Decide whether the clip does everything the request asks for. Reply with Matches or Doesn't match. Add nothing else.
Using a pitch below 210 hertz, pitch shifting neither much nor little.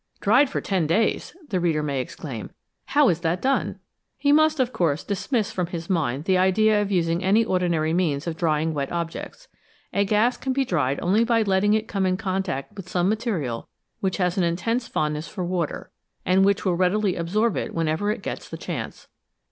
Matches